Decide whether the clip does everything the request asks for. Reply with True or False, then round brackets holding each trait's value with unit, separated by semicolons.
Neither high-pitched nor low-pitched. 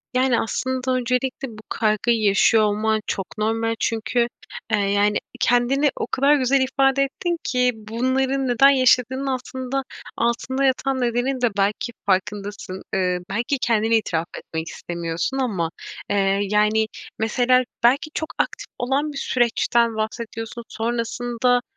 False (235 Hz)